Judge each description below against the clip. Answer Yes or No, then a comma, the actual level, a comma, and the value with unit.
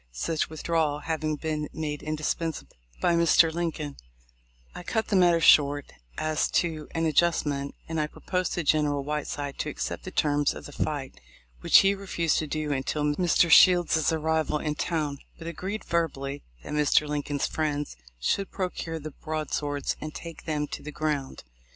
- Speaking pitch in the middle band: Yes, medium, 155 Hz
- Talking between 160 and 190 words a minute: Yes, average, 165 wpm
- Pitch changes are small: Yes, narrow, 2.1 semitones